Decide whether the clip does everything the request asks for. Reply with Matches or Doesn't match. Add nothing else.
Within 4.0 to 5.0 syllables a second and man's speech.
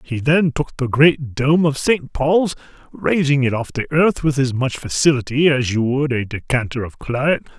Matches